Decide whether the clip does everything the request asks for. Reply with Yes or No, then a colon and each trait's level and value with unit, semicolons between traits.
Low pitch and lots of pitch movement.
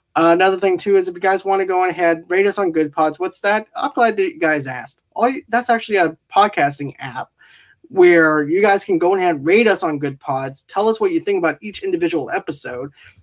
No: high, 190 Hz; wide, 7.0 semitones